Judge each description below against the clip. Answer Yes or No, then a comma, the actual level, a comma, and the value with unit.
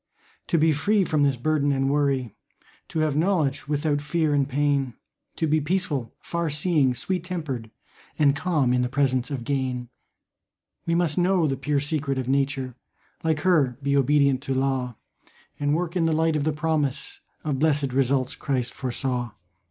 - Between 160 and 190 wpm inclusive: Yes, average, 170 wpm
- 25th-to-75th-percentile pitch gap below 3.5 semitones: Yes, average, 2.9 semitones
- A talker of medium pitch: Yes, medium, 145 Hz